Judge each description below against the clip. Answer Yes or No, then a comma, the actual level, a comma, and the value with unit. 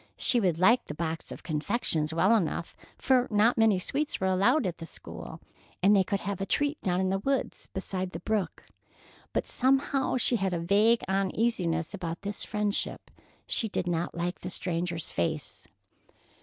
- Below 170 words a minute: No, average, 175 wpm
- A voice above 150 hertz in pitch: Yes, high, 190 Hz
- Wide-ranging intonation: No, average, 4.6 semitones